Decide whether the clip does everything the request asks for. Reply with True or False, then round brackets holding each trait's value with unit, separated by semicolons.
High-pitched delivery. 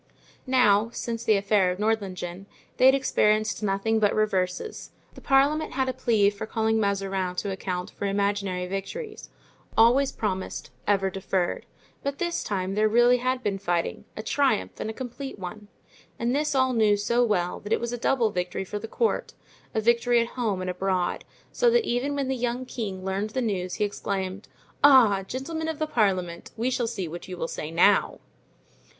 True (215 Hz)